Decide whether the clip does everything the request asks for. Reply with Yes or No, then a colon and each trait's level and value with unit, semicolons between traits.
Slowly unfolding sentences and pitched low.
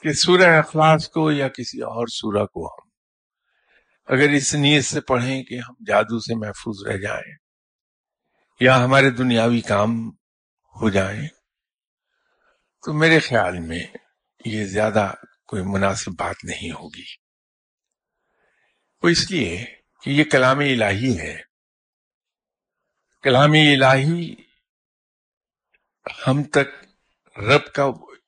Yes: slow, 110 wpm; low, 130 Hz